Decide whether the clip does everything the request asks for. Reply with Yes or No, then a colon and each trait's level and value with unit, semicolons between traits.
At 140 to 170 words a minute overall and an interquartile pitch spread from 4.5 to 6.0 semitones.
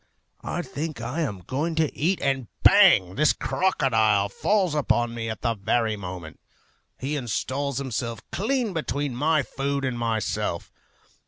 Yes: average, 145 wpm; average, 5.2 semitones